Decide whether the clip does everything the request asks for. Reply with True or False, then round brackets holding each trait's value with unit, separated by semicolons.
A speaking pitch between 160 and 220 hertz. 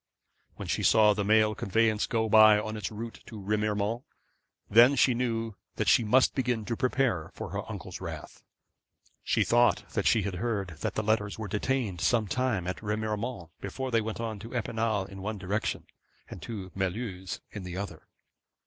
False (110 Hz)